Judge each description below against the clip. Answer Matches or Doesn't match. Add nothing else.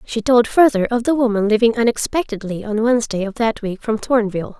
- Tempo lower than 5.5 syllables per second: Doesn't match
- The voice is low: Doesn't match